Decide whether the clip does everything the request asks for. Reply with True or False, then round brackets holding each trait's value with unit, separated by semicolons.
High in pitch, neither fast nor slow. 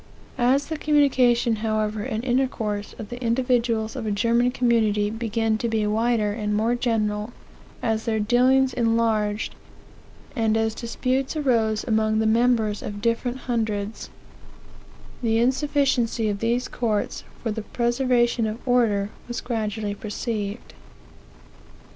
False (230 Hz; 130 wpm)